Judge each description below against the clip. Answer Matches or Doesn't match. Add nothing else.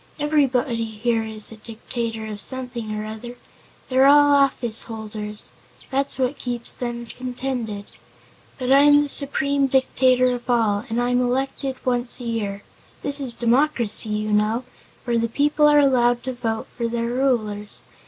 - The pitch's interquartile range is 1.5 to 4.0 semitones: Matches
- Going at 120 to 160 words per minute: Matches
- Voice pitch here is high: Matches